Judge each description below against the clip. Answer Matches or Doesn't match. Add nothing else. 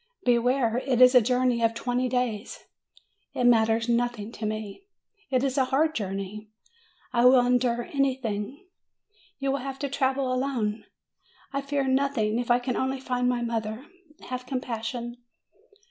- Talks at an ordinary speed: Matches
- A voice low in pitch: Doesn't match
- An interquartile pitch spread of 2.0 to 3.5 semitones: Matches